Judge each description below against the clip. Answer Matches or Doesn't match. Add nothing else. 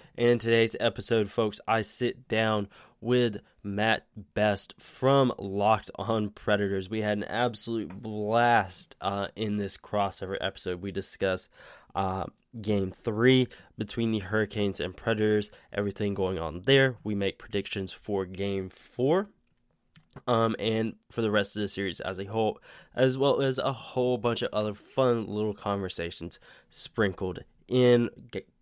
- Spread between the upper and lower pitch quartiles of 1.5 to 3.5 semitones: Matches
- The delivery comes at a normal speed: Matches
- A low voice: Matches